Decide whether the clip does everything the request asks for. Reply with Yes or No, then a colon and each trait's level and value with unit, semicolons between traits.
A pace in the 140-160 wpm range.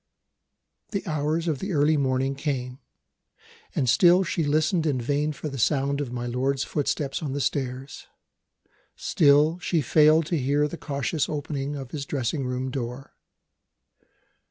Yes: average, 150 wpm